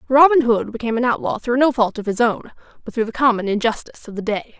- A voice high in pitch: Yes, high, 235 Hz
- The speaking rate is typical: No, fast, 250 wpm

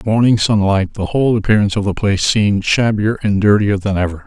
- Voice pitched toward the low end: Yes, low, 105 Hz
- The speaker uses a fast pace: Yes, fast, 225 wpm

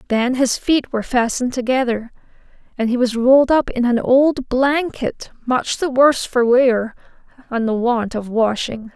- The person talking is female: Yes, female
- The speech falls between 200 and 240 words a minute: No, average, 170 wpm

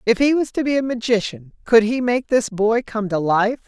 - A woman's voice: Yes, female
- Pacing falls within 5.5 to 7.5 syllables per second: No, 5.1 syllables/s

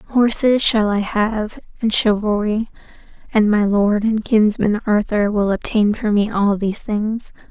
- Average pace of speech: Yes, average, 150 wpm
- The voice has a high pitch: Yes, high, 210 Hz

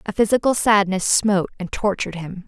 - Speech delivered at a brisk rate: No, average, 170 wpm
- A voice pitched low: No, high, 200 Hz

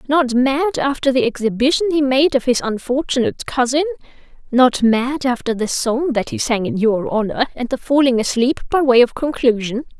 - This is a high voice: Yes, very high, 255 Hz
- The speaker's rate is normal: Yes, average, 180 wpm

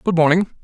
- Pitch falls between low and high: Yes, medium, 175 Hz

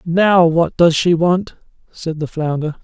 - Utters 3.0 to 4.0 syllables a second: Yes, 3.8 syllables/s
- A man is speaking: Yes, male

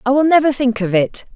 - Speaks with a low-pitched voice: No, very high, 250 Hz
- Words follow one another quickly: Yes, fast, 265 wpm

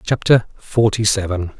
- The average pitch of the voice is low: Yes, low, 105 Hz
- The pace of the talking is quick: No, slow, 115 wpm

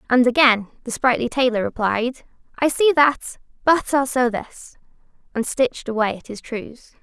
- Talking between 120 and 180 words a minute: Yes, average, 160 wpm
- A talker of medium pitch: No, very high, 250 Hz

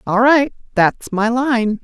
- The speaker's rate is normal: No, slow, 130 wpm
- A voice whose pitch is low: No, high, 235 Hz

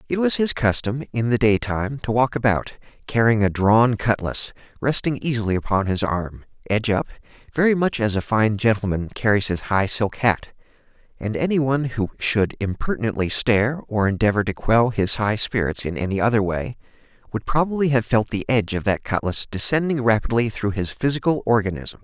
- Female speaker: No, male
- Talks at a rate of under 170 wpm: No, average, 175 wpm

